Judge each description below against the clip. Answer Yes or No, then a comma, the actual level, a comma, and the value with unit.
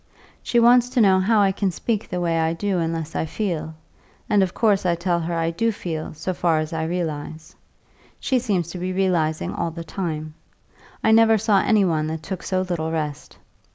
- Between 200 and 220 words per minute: Yes, fast, 205 wpm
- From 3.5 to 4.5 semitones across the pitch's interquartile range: Yes, average, 3.8 semitones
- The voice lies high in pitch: No, medium, 175 Hz